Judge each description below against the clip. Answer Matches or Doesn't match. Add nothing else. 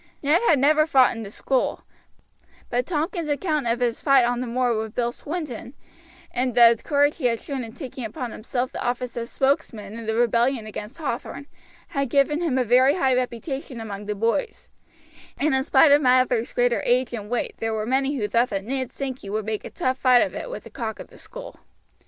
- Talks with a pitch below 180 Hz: Doesn't match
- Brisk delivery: Matches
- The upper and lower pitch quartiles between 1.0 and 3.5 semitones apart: Matches